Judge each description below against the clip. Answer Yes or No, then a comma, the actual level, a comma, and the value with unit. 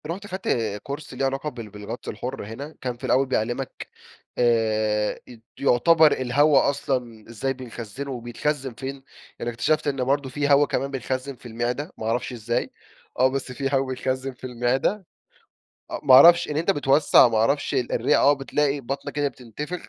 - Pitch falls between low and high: No, low, 130 Hz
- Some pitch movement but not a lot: Yes, average, 3.0 semitones